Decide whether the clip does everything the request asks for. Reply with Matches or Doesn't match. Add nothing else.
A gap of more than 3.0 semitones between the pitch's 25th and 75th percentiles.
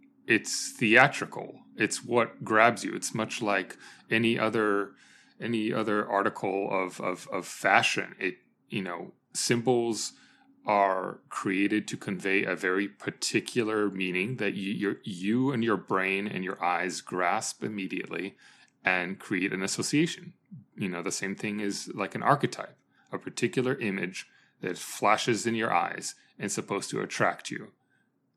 Matches